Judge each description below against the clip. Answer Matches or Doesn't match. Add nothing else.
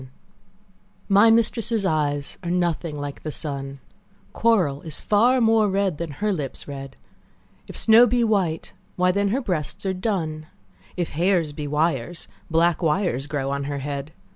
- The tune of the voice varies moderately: Doesn't match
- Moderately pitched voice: Matches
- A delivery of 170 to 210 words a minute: Doesn't match